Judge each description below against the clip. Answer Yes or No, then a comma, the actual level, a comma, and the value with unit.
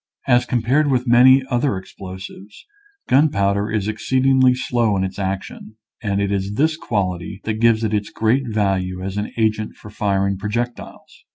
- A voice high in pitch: No, low, 110 Hz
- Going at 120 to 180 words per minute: Yes, average, 160 wpm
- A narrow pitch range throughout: No, average, 3.7 semitones